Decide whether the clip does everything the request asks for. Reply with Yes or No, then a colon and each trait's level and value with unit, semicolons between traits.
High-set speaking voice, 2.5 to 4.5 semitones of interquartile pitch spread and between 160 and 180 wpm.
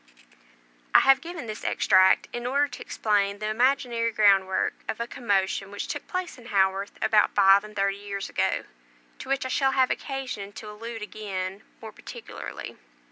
Yes: high, 215 Hz; average, 4.2 semitones; average, 170 wpm